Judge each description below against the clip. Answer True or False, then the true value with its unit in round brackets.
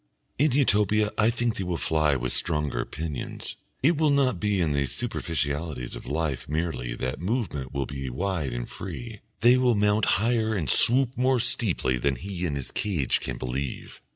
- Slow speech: False (180 wpm)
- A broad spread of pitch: True (8.2 semitones)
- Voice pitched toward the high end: False (85 Hz)